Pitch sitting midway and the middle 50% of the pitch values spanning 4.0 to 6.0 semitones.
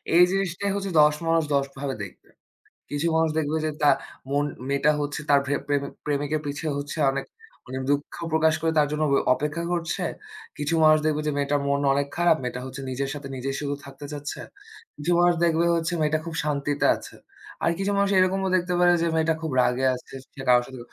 No: medium, 150 Hz; average, 2.7 semitones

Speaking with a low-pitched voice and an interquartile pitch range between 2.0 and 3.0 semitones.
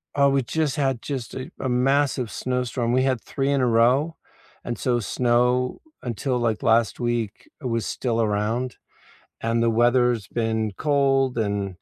Yes: low, 125 Hz; narrow, 2.4 semitones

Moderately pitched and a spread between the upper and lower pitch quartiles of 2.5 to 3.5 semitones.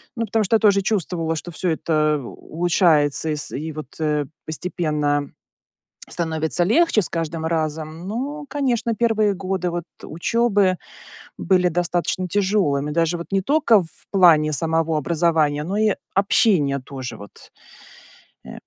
No: medium, 170 Hz; average, 4.4 semitones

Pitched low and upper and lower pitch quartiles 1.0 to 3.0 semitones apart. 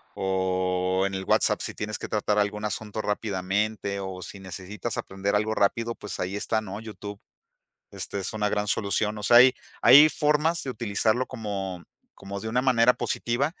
Yes: low, 105 Hz; narrow, 2.6 semitones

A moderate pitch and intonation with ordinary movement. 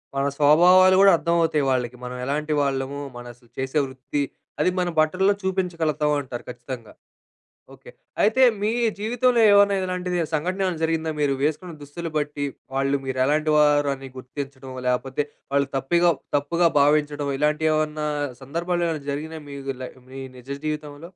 Yes: medium, 150 Hz; average, 3.8 semitones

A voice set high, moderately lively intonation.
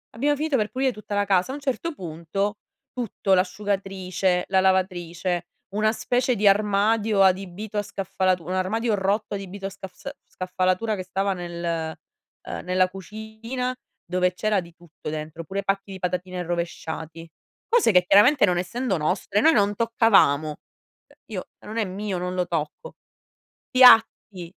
Yes: high, 195 Hz; average, 3.2 semitones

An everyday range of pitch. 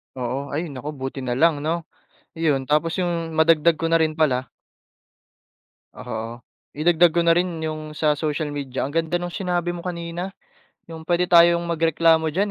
No: narrow, 2.1 semitones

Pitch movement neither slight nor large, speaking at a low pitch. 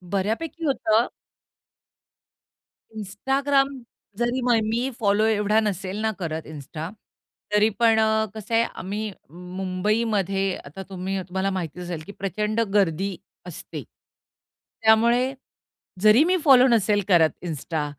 No: average, 3.5 semitones; high, 210 Hz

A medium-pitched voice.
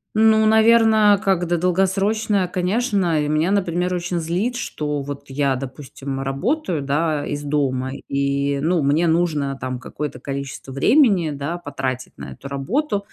Yes: medium, 165 Hz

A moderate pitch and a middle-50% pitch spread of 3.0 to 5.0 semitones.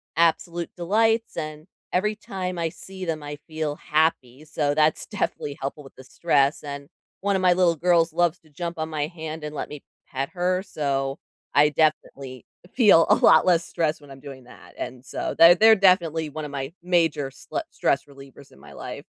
Yes: medium, 155 Hz; average, 3.5 semitones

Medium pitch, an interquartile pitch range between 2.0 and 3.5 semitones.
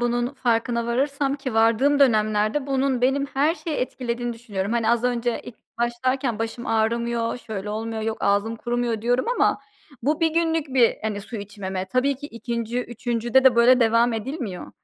No: high, 235 Hz; average, 2.7 semitones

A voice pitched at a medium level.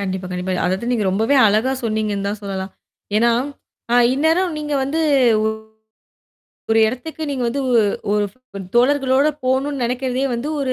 No: high, 245 Hz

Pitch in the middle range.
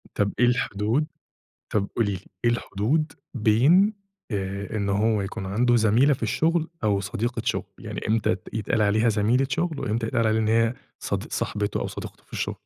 No: low, 110 Hz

